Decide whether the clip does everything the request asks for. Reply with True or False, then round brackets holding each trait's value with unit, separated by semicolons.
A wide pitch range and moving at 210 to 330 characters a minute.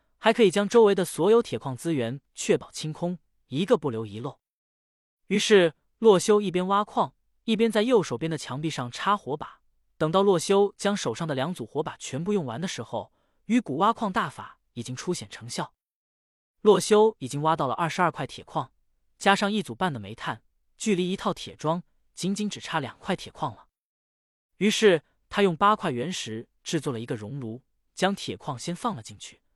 True (7.9 semitones; 270 characters per minute)